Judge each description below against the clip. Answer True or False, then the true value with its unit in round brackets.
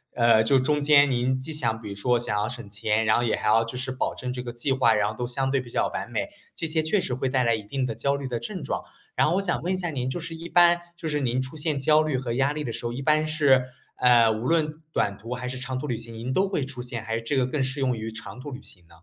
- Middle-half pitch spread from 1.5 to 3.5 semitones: False (4.0 semitones)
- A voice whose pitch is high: False (130 Hz)